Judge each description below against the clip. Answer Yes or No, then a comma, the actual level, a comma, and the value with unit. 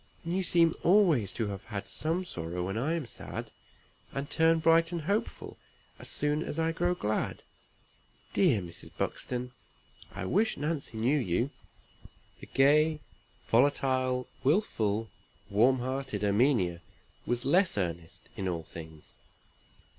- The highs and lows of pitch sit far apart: Yes, wide, 7.9 semitones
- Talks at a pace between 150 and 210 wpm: No, slow, 135 wpm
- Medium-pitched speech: No, low, 130 Hz